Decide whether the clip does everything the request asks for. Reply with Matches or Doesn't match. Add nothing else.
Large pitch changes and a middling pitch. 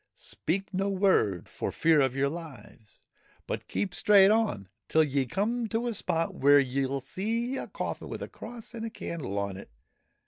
Matches